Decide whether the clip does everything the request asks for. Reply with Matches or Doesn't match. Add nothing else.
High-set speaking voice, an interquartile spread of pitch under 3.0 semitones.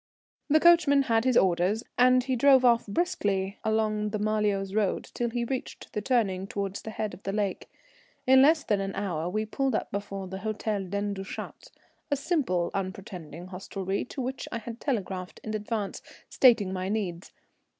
Doesn't match